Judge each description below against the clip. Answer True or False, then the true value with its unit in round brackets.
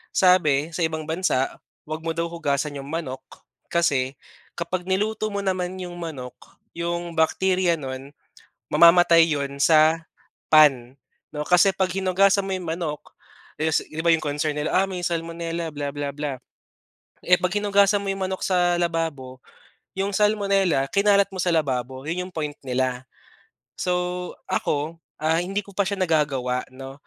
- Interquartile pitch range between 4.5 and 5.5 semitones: False (4.1 semitones)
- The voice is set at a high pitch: False (165 Hz)